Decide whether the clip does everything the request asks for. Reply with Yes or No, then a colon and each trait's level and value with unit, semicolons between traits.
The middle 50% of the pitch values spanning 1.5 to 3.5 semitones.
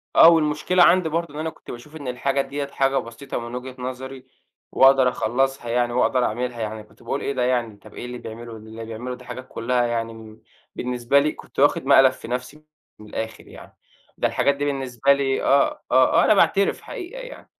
Yes: average, 2.9 semitones